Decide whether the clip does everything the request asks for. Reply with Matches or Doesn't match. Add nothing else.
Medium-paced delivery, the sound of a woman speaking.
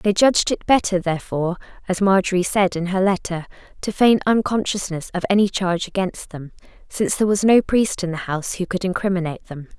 Matches